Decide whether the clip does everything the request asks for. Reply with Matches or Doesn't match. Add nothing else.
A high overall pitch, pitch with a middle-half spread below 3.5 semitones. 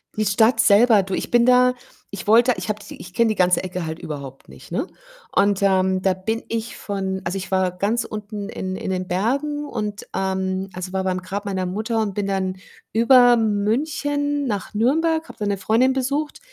Doesn't match